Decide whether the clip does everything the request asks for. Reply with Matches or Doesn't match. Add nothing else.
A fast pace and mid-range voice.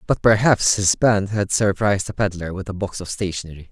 Doesn't match